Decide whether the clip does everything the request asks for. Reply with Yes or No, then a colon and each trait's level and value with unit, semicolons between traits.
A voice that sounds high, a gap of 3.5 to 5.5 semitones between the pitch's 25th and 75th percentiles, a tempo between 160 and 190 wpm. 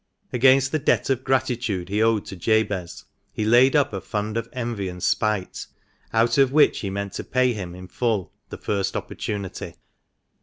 No: low, 110 Hz; average, 4.1 semitones; average, 180 wpm